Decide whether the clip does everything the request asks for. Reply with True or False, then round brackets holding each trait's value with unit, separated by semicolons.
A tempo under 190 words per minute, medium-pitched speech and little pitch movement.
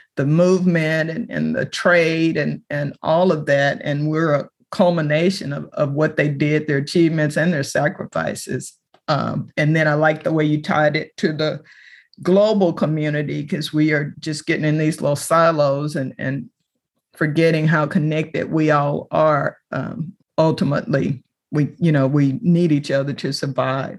True (170 wpm; 155 Hz; 2.2 semitones)